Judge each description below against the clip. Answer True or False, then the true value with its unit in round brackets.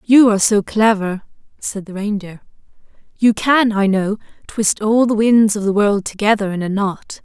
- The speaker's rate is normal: True (180 wpm)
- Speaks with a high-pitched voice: True (210 Hz)